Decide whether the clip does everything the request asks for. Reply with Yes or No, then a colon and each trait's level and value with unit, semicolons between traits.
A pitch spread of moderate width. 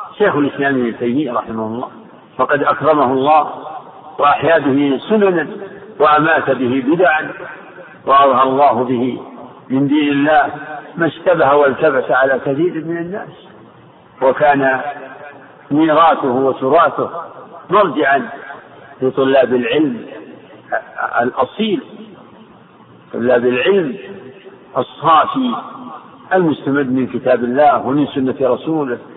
Yes: average, 3.2 semitones